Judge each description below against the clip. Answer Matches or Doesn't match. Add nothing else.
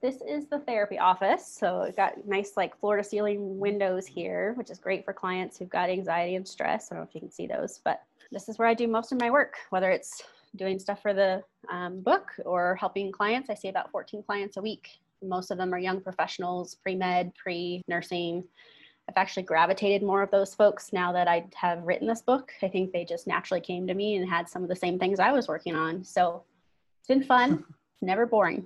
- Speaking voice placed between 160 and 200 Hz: Matches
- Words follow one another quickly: Matches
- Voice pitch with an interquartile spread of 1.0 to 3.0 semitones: Matches